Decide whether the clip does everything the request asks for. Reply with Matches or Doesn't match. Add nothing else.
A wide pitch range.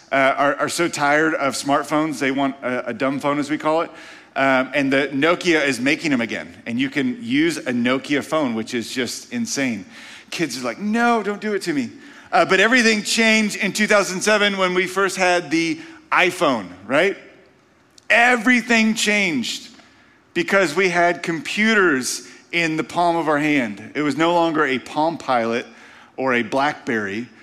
Matches